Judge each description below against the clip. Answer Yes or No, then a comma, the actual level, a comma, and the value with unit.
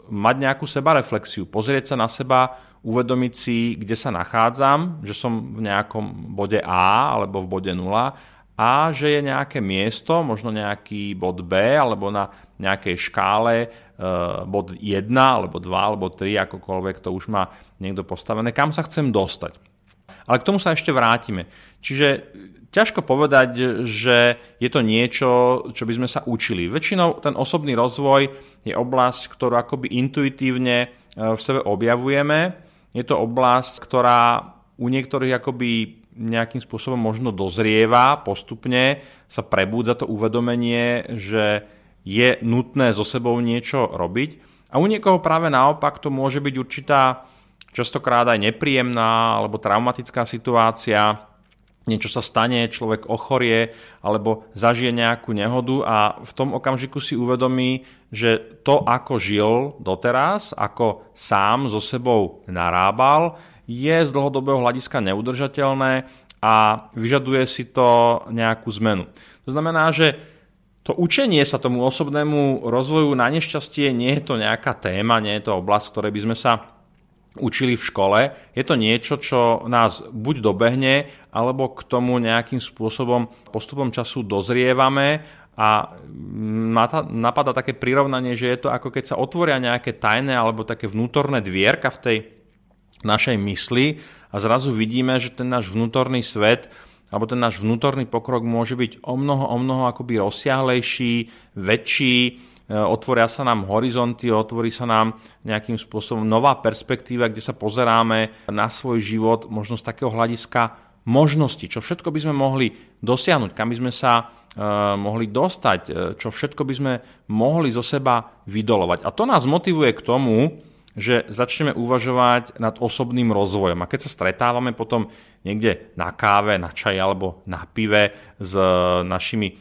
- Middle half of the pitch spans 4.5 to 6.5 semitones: No, average, 3.2 semitones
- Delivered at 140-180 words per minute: Yes, average, 145 wpm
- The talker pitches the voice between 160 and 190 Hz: No, low, 120 Hz